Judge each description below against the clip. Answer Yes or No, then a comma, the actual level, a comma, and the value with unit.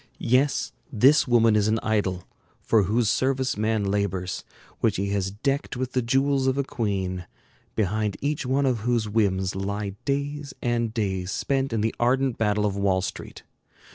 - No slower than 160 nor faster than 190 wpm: Yes, average, 170 wpm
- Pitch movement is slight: No, average, 4.6 semitones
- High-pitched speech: No, low, 110 Hz